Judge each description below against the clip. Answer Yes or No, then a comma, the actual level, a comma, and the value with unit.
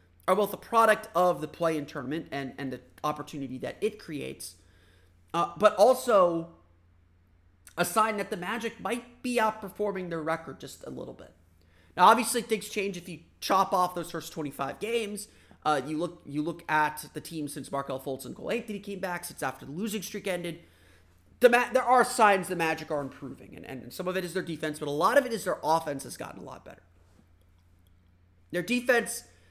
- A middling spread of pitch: No, wide, 7.8 semitones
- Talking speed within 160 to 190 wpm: No, fast, 205 wpm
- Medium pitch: Yes, medium, 165 Hz